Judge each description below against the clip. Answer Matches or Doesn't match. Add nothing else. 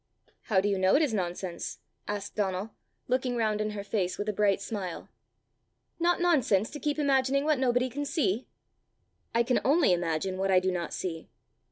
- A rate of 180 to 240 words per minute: Matches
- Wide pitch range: Matches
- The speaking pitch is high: Matches